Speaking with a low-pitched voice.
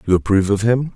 Yes: low, 105 Hz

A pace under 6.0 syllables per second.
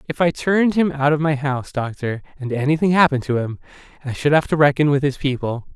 No: 6.3 syllables/s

